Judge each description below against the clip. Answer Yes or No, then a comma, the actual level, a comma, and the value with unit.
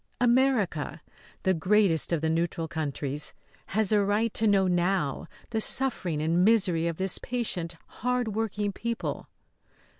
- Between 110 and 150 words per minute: Yes, average, 140 wpm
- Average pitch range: Yes, average, 5.0 semitones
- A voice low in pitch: No, high, 190 Hz